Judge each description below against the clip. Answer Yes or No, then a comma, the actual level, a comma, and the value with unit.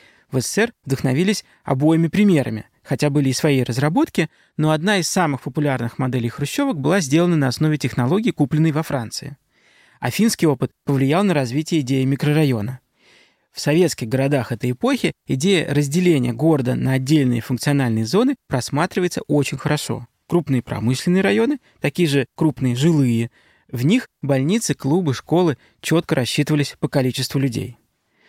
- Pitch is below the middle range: No, medium, 145 Hz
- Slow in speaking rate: No, average, 140 wpm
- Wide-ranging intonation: No, average, 4.2 semitones